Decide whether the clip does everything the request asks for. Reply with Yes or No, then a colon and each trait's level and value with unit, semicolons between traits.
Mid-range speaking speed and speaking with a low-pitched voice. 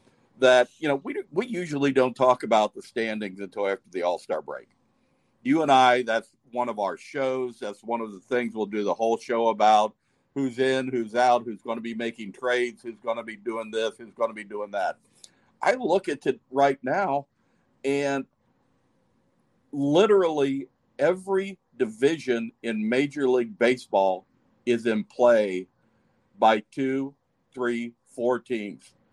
Yes: average, 155 wpm; low, 120 Hz